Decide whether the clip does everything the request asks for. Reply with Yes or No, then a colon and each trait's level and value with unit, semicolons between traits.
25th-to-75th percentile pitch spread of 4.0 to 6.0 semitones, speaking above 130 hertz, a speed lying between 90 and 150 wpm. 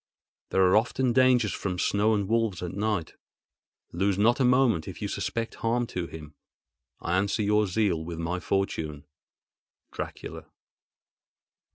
No: average, 4.5 semitones; low, 100 Hz; average, 140 wpm